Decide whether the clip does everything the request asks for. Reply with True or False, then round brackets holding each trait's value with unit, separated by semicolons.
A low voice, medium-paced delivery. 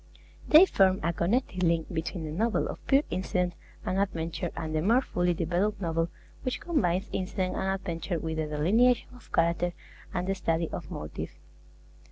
False (180 Hz; 170 wpm)